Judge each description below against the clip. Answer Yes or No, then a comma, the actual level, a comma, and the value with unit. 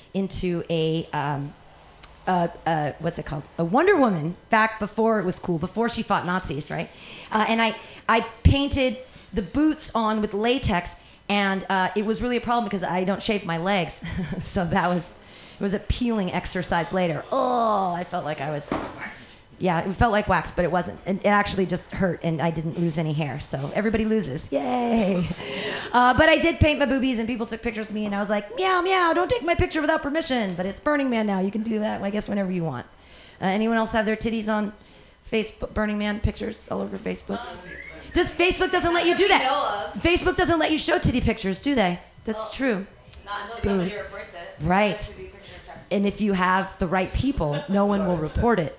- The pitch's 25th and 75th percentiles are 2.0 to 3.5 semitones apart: No, average, 4.5 semitones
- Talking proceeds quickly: Yes, fast, 210 wpm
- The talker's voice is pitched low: No, high, 205 Hz